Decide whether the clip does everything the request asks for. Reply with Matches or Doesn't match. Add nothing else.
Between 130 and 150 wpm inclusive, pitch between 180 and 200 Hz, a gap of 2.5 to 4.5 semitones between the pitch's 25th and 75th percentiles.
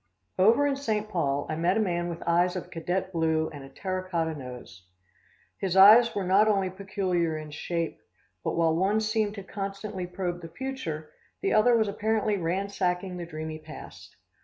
Doesn't match